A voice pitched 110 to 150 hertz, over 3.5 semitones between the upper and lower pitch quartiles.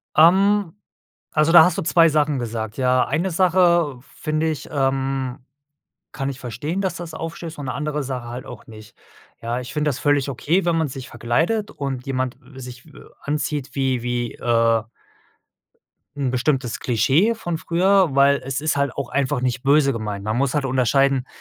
Yes: medium, 140 Hz; average, 4.0 semitones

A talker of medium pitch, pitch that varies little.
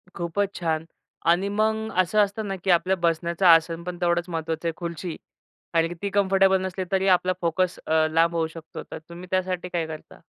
Yes: medium, 175 Hz; narrow, 2.3 semitones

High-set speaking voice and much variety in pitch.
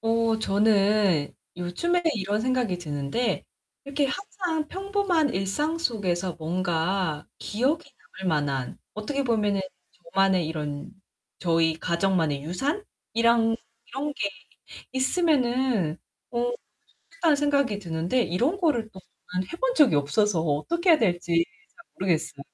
Yes: high, 210 Hz; wide, 8.3 semitones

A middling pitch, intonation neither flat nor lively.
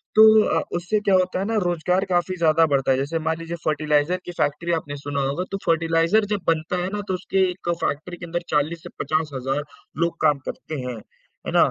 Yes: medium, 165 Hz; average, 3.3 semitones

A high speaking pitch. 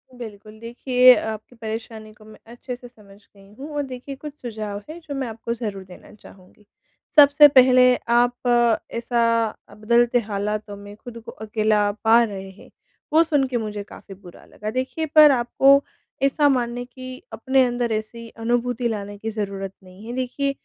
Yes: high, 235 Hz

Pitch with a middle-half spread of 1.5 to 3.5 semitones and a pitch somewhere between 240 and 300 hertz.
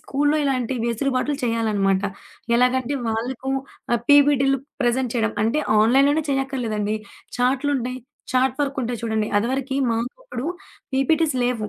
Yes: average, 2.9 semitones; very high, 255 Hz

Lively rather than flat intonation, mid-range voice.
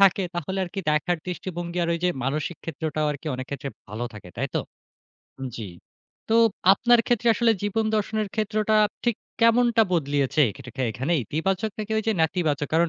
Yes: wide, 6.6 semitones; medium, 175 Hz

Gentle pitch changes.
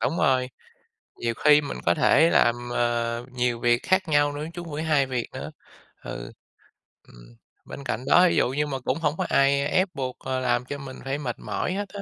No: average, 3.6 semitones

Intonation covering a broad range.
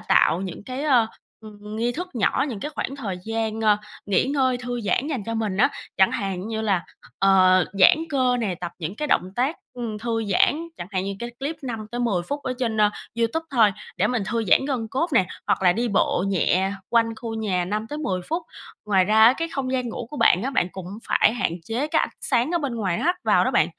No: average, 4.7 semitones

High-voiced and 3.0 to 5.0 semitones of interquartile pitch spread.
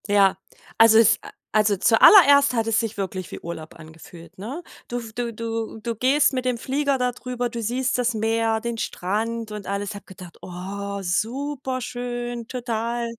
Yes: high, 230 Hz; average, 3.4 semitones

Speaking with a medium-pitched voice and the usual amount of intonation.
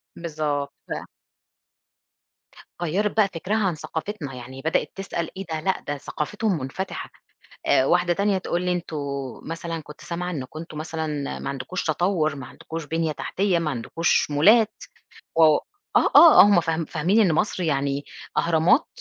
Yes: medium, 165 Hz; average, 3.5 semitones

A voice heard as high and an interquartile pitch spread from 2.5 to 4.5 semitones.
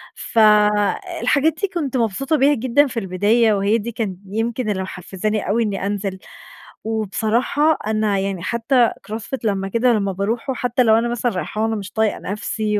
Yes: high, 220 Hz; average, 3.0 semitones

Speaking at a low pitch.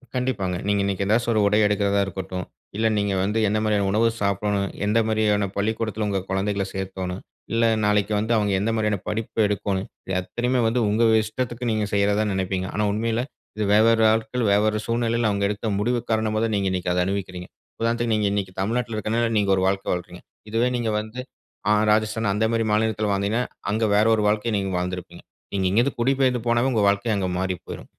Yes: low, 105 Hz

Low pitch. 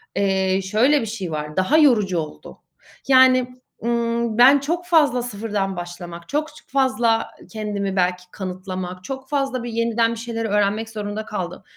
No: high, 225 Hz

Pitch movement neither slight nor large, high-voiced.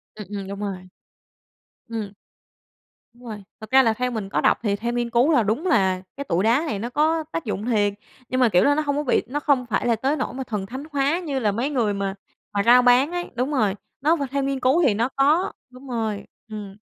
Yes: average, 5.0 semitones; high, 240 Hz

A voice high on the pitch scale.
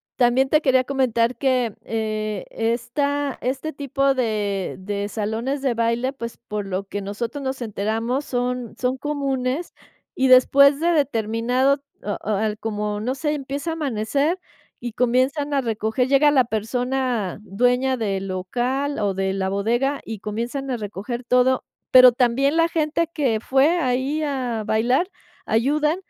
Yes: very high, 250 Hz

